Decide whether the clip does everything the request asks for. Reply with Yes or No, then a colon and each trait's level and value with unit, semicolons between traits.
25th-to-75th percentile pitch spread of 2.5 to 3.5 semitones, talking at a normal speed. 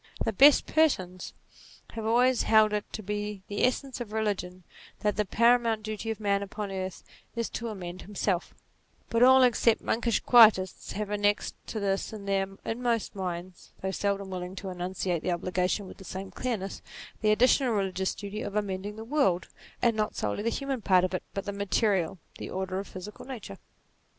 Yes: average, 3.1 semitones; average, 185 wpm